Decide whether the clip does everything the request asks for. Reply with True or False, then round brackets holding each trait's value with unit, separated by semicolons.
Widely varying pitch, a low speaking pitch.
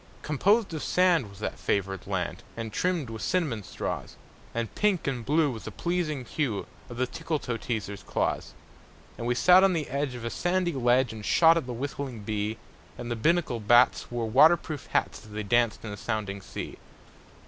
True (6.6 semitones; 120 Hz)